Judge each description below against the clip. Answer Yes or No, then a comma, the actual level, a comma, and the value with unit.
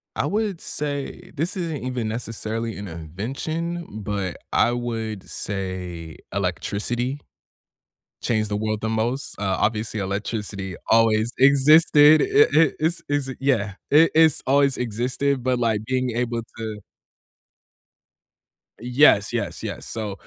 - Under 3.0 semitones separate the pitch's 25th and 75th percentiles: No, average, 5.0 semitones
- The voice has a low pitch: Yes, low, 120 Hz